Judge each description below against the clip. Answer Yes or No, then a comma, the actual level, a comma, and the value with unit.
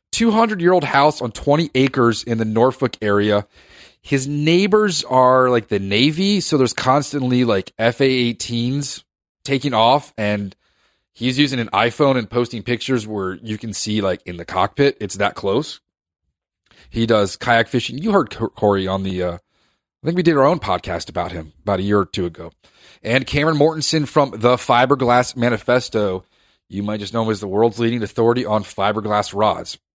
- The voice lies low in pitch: Yes, low, 120 Hz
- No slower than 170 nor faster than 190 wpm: Yes, average, 180 wpm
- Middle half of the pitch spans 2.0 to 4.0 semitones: No, average, 4.8 semitones